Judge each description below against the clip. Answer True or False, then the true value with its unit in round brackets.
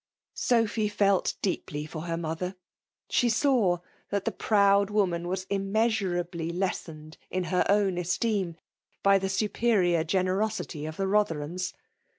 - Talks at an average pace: True (145 wpm)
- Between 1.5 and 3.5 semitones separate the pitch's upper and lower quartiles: True (3.1 semitones)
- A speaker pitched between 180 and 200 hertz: True (190 Hz)